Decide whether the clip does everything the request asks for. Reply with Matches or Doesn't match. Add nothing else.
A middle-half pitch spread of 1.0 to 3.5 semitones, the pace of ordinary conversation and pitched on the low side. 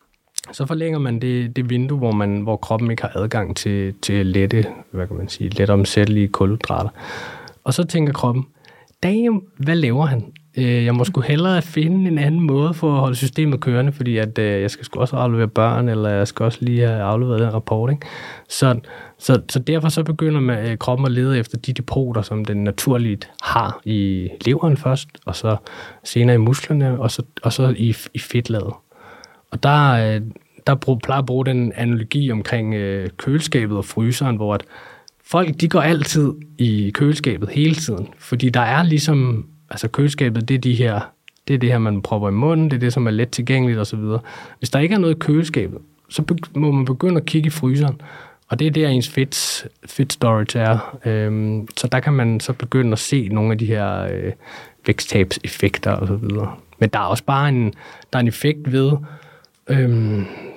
Doesn't match